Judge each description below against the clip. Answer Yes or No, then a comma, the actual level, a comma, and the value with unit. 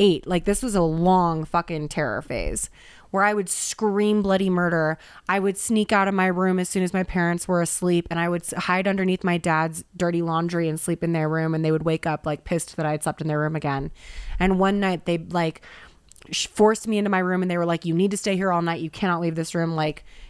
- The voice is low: No, medium, 175 Hz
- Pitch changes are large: No, average, 2.7 semitones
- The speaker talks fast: Yes, fast, 250 wpm